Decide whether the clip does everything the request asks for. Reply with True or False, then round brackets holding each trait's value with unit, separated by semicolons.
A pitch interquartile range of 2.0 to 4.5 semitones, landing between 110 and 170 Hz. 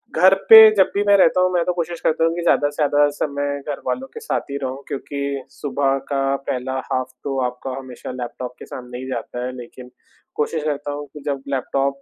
True (2.8 semitones; 140 Hz)